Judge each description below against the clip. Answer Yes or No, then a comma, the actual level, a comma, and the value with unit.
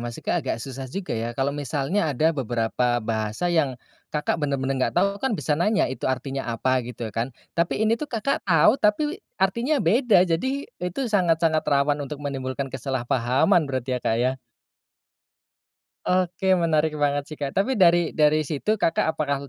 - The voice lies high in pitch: No, medium, 150 Hz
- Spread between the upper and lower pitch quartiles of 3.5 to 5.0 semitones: No, wide, 5.5 semitones